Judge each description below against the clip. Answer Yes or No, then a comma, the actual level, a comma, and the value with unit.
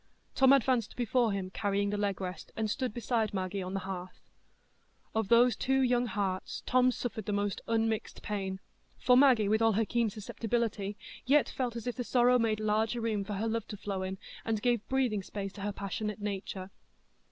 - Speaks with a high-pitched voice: Yes, high, 215 Hz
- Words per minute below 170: No, average, 195 wpm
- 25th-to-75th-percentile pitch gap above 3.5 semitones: No, average, 3.2 semitones